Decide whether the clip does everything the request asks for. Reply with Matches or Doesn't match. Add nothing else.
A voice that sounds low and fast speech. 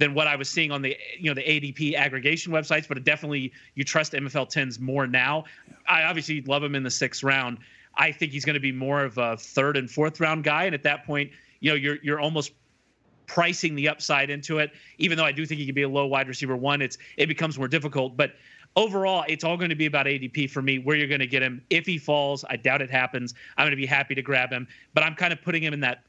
Doesn't match